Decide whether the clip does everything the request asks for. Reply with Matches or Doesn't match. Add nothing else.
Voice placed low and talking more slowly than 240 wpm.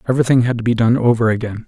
Doesn't match